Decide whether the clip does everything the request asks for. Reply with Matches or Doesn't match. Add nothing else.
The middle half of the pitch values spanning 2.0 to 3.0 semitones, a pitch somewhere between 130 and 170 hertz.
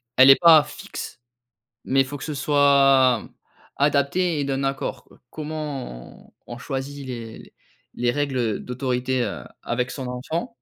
Matches